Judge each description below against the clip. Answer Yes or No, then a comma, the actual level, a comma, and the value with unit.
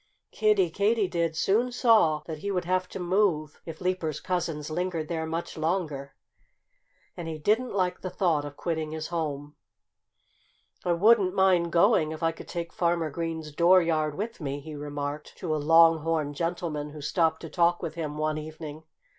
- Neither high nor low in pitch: Yes, medium, 165 Hz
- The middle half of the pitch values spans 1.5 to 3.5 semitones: Yes, average, 2.8 semitones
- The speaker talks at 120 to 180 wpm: Yes, average, 170 wpm